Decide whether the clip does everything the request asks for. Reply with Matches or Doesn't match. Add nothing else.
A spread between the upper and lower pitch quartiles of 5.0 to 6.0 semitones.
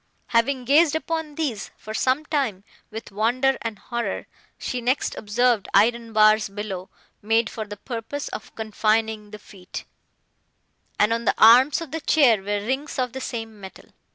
Doesn't match